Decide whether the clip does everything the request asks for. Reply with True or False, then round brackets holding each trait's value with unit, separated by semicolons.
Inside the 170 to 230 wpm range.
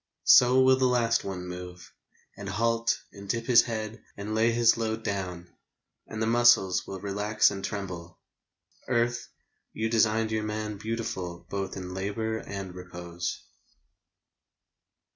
False (140 wpm)